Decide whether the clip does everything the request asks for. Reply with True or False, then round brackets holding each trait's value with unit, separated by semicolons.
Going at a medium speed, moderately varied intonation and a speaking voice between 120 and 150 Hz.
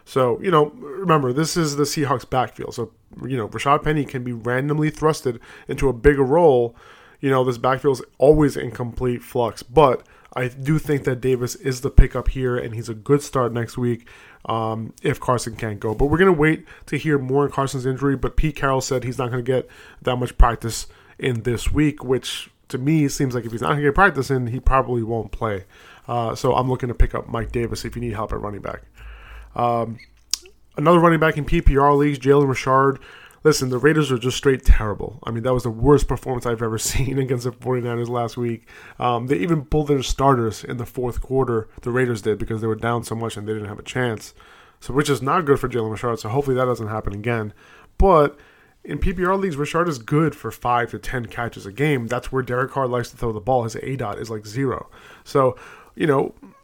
False (225 wpm; 3.2 semitones; 125 Hz)